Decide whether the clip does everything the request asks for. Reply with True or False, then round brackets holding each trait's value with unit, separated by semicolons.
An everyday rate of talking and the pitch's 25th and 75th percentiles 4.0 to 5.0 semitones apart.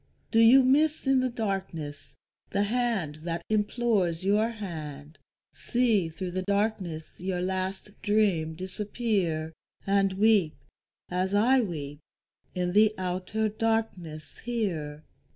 False (115 wpm; 4.6 semitones)